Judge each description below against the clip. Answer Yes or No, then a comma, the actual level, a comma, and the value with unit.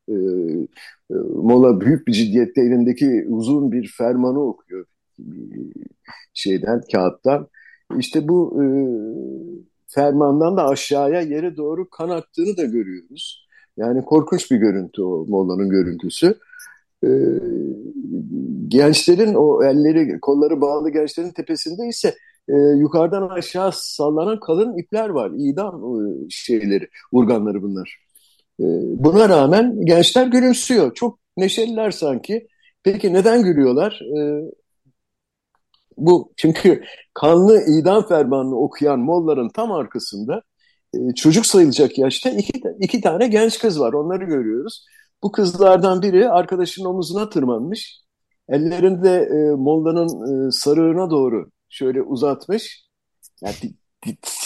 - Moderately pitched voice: Yes, medium, 170 Hz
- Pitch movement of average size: No, wide, 7.9 semitones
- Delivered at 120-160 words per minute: No, average, 110 wpm